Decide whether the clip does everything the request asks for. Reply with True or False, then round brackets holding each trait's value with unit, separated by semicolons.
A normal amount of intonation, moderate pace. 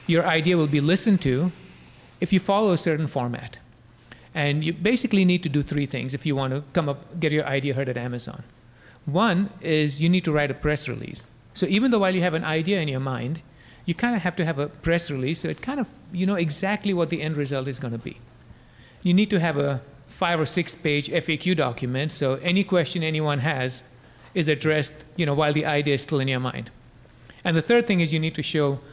False (4.4 semitones; 235 wpm)